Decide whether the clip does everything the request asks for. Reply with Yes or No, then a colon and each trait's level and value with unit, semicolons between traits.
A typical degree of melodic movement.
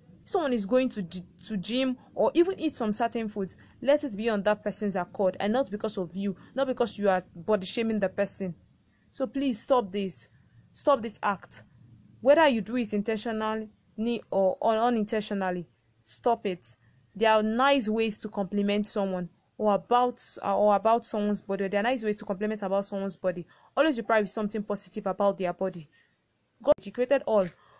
Yes: average, 3.4 semitones